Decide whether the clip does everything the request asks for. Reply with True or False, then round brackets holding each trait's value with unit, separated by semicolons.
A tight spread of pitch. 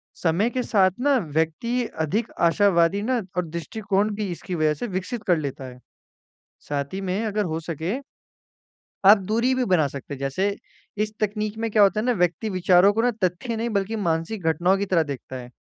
False (4.6 semitones)